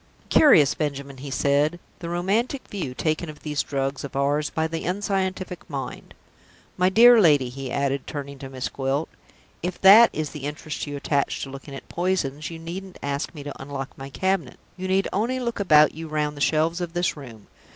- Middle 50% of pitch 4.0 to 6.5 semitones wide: Yes, average, 4.6 semitones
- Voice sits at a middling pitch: Yes, medium, 155 Hz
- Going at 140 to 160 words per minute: No, average, 195 wpm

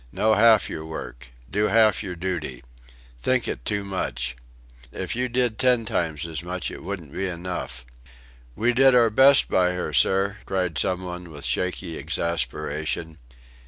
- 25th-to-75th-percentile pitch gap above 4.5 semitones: Yes, average, 5.0 semitones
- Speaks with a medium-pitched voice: No, very low, 90 Hz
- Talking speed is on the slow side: No, average, 160 wpm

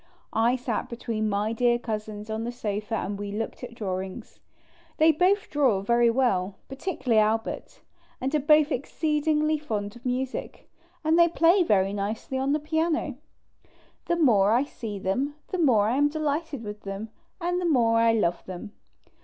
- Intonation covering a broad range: Yes, wide, 6.0 semitones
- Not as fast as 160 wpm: No, average, 170 wpm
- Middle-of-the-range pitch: No, high, 240 Hz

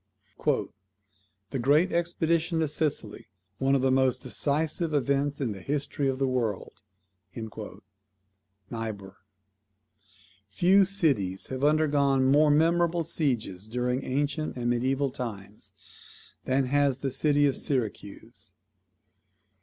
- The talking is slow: Yes, slow, 110 wpm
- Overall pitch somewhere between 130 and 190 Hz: Yes, low, 135 Hz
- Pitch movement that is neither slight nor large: Yes, average, 4.9 semitones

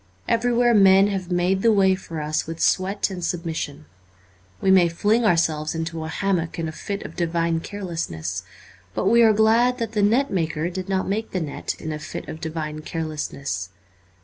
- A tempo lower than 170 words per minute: No, average, 190 wpm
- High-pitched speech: No, medium, 180 Hz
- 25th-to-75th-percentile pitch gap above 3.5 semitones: Yes, average, 4.0 semitones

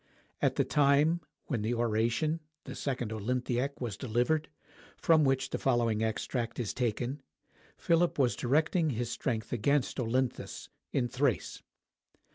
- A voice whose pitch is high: No, low, 125 Hz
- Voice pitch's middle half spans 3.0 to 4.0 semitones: Yes, average, 3.5 semitones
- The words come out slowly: Yes, slow, 130 wpm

